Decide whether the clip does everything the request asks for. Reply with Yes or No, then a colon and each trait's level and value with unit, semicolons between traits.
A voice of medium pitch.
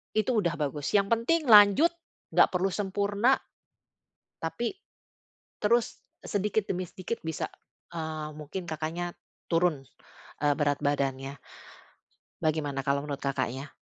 Yes: medium, 170 Hz